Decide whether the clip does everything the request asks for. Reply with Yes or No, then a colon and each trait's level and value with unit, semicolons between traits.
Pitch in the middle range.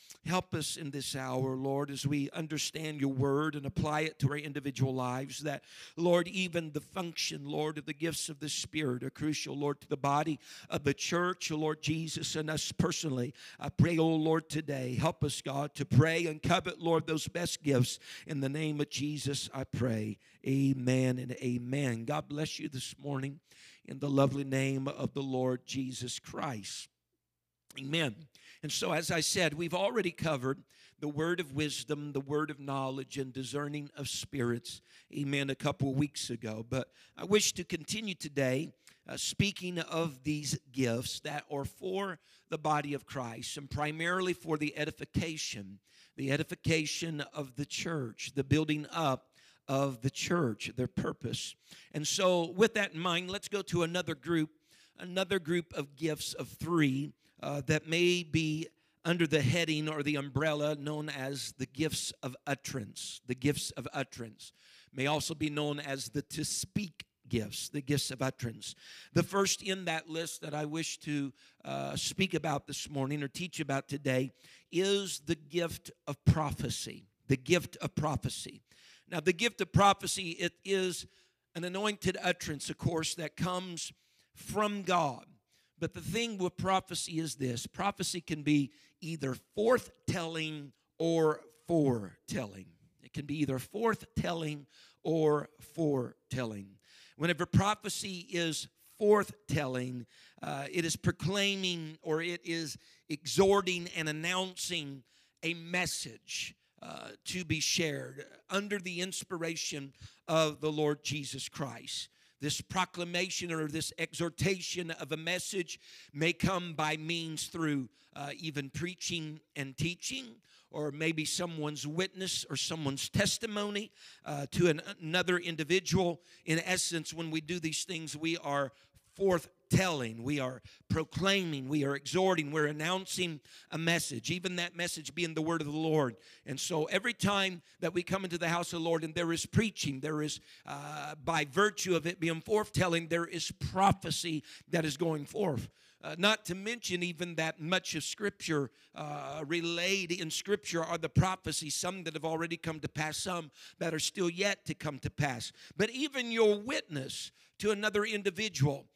Yes: medium, 155 Hz